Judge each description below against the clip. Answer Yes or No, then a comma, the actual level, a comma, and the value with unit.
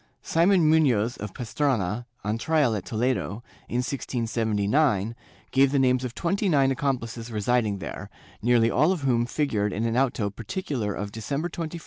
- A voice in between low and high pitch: No, low, 120 Hz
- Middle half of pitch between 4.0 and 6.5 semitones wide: Yes, average, 4.3 semitones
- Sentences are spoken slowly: No, average, 160 wpm